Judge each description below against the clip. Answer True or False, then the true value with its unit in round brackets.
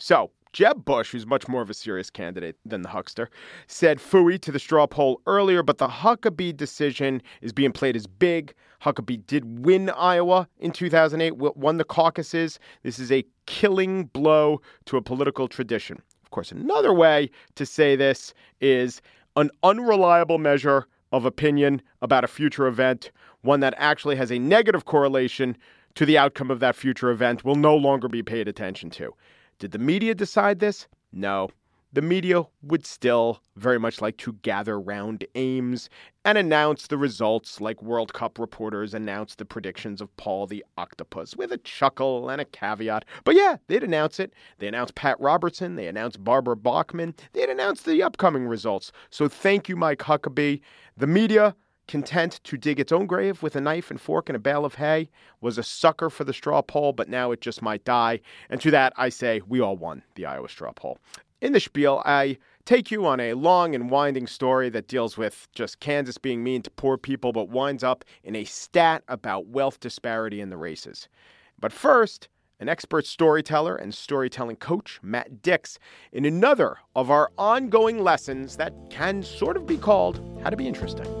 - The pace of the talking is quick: False (185 wpm)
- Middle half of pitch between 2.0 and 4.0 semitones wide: False (5.1 semitones)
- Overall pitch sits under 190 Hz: True (140 Hz)